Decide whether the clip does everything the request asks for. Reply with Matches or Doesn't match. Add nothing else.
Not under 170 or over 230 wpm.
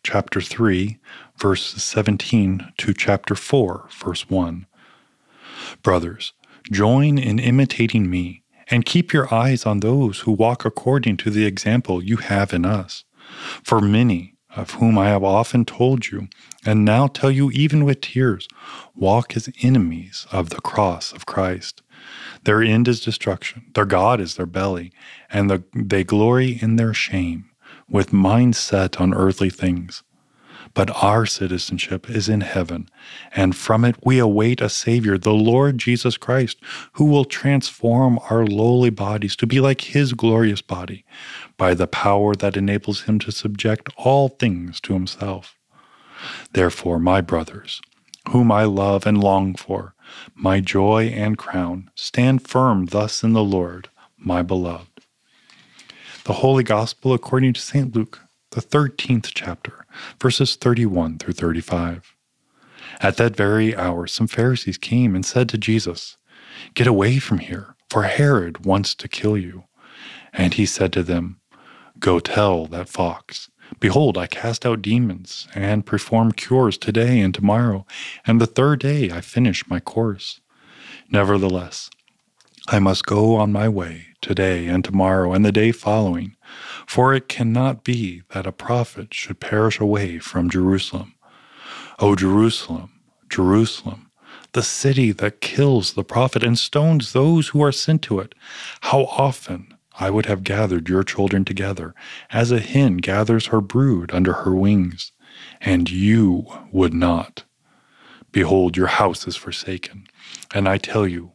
Doesn't match